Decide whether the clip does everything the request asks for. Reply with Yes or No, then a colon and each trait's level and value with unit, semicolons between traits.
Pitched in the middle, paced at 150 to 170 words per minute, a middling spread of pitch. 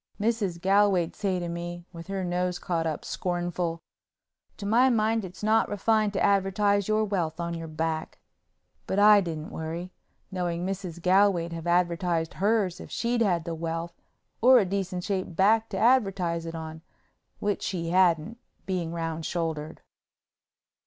Yes: medium, 180 Hz; average, 155 wpm; average, 3.3 semitones